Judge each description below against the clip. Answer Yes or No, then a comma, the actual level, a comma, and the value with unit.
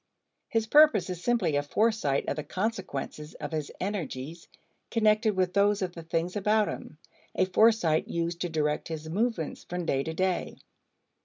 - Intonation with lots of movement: No, average, 5.0 semitones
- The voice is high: No, medium, 180 Hz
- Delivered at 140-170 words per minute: Yes, average, 165 wpm